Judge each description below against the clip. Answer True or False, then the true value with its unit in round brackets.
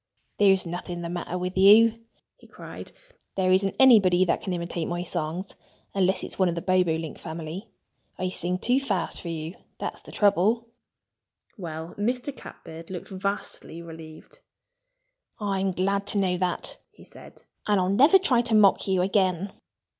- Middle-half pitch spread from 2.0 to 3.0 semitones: True (2.6 semitones)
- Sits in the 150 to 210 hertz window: True (185 Hz)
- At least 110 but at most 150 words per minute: False (160 wpm)